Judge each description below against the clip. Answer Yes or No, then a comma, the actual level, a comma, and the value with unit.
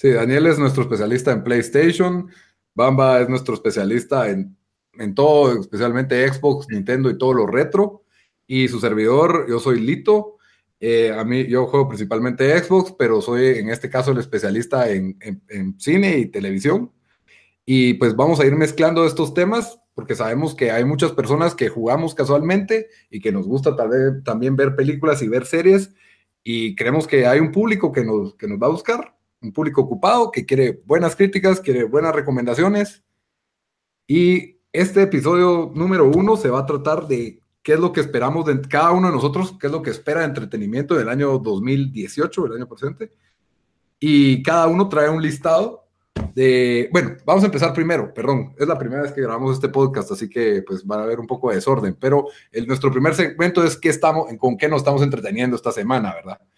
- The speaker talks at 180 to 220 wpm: Yes, fast, 190 wpm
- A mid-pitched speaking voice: Yes, medium, 145 Hz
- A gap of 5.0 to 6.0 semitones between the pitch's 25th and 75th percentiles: Yes, wide, 5.4 semitones